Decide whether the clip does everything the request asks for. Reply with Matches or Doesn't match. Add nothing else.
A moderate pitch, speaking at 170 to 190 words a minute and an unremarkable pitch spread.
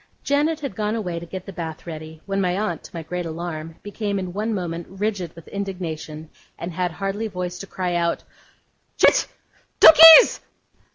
Matches